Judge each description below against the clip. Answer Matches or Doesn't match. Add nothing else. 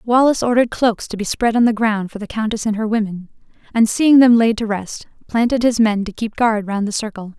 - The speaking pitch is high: Matches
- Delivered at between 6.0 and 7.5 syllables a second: Doesn't match